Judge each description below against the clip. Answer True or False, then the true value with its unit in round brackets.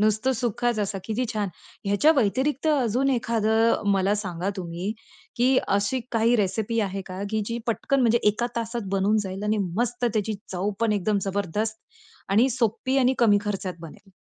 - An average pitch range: True (3.1 semitones)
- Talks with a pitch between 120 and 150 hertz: False (215 Hz)